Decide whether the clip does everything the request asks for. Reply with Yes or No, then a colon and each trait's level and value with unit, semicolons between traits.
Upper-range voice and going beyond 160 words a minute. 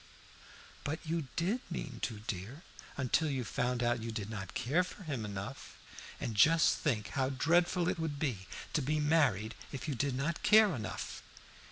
No: medium, 140 Hz; average, 175 wpm